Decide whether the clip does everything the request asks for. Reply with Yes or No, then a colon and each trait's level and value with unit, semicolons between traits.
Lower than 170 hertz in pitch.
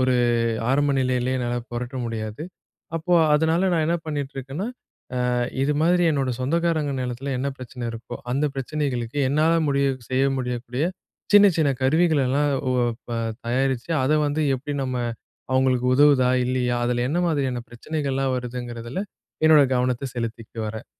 Yes: low, 135 Hz